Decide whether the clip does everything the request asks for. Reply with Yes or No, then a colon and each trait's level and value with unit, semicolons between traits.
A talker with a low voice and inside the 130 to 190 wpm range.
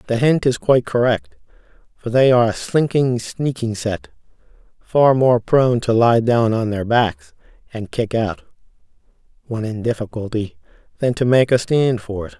Yes: low, 120 Hz; average, 165 wpm